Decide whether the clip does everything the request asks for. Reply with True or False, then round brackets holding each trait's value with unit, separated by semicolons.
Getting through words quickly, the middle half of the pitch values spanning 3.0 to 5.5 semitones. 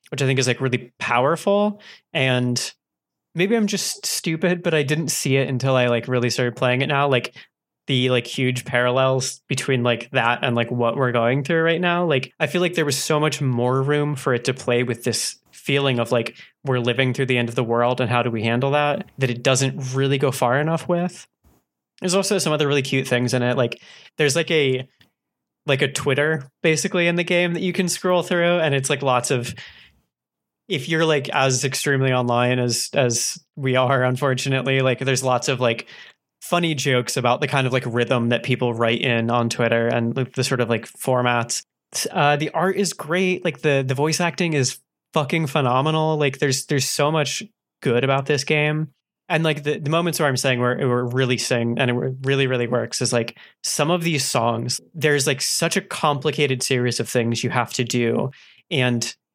True (210 wpm; 3.7 semitones)